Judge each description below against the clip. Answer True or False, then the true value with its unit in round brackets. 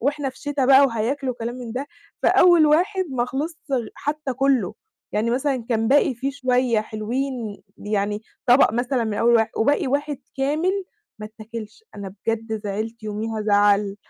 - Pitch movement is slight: False (4.2 semitones)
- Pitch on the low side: False (245 Hz)